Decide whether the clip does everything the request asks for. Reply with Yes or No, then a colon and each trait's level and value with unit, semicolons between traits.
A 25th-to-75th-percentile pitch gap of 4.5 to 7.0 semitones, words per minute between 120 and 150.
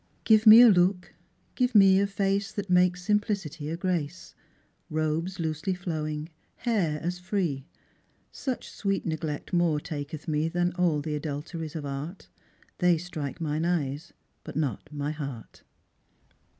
No: average, 3.7 semitones; average, 140 wpm